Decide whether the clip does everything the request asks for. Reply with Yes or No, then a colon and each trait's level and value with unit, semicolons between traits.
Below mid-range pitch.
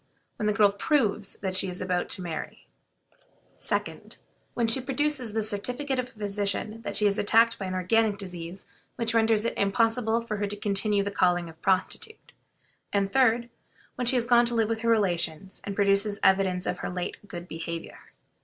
No: high, 205 Hz